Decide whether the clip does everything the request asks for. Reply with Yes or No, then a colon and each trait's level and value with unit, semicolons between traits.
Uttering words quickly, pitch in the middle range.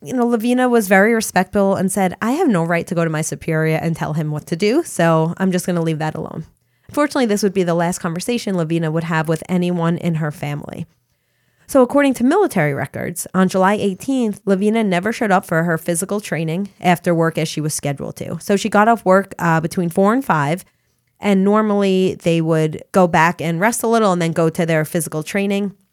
Yes: fast, 220 wpm; medium, 180 Hz